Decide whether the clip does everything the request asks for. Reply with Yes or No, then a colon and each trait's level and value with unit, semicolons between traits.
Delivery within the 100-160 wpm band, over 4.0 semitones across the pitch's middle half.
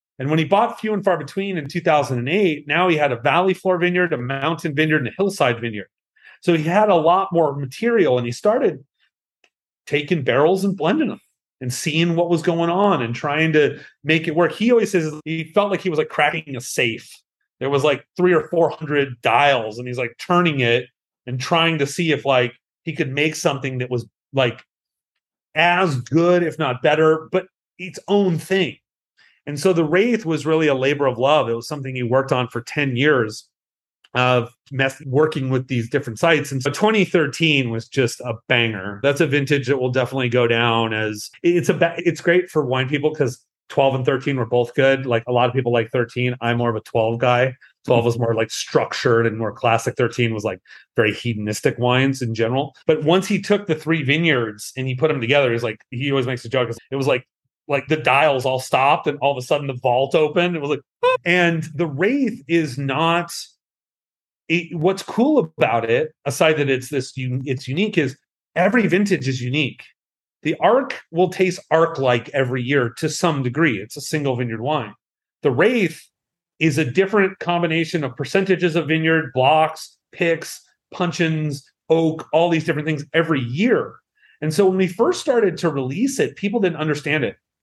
No: fast, 205 wpm; average, 5.0 semitones